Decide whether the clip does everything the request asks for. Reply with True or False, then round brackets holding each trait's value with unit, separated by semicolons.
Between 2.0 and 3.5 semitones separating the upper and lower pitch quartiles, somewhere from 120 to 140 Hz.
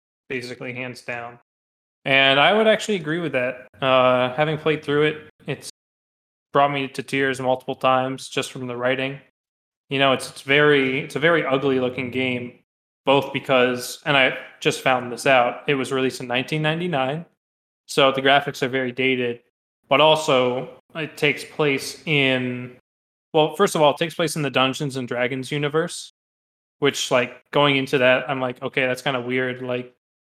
True (2.4 semitones; 130 Hz)